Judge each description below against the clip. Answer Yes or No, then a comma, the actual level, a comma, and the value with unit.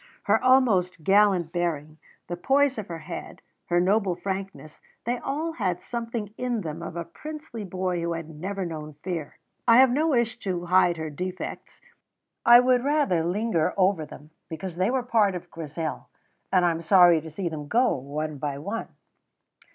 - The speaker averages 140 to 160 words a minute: No, average, 175 wpm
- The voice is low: No, medium, 185 Hz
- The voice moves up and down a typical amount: No, wide, 5.7 semitones